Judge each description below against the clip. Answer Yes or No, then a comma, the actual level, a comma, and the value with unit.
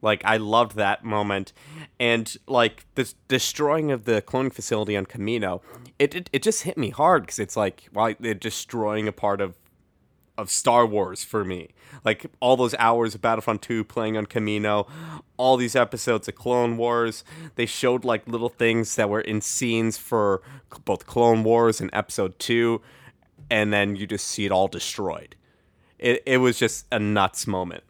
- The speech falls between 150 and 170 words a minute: No, average, 180 wpm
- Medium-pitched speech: No, low, 115 Hz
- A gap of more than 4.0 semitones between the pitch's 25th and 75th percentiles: No, average, 2.9 semitones